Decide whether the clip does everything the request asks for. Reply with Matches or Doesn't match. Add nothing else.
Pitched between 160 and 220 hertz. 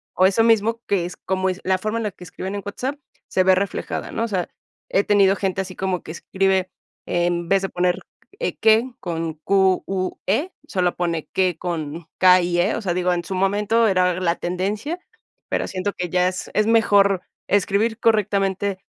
Matches